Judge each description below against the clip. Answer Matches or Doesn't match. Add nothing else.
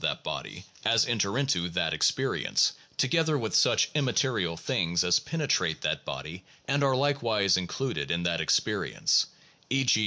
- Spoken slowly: Matches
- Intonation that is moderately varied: Doesn't match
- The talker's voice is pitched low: Matches